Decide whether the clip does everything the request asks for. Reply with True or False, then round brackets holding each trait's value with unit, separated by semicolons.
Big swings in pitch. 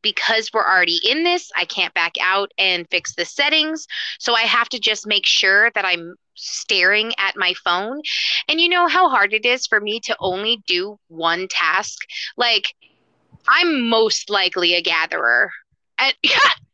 True (7.7 semitones)